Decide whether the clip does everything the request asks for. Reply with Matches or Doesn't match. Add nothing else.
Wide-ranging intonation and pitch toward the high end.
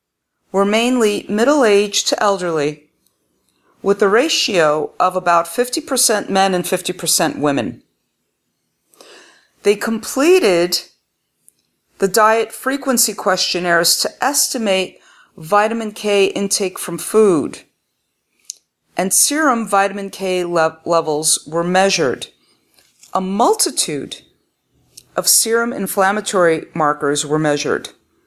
Doesn't match